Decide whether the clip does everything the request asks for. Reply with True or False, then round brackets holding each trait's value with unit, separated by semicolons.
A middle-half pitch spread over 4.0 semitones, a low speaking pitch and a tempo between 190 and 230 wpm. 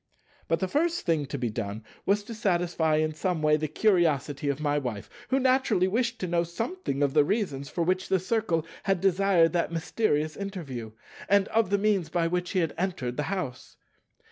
False (4.9 semitones; 175 Hz; 195 wpm)